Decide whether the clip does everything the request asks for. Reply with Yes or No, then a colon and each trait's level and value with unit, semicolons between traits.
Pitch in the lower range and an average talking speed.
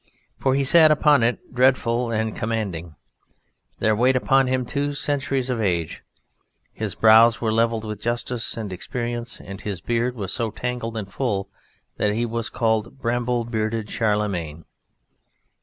Yes: low, 115 Hz; average, 150 wpm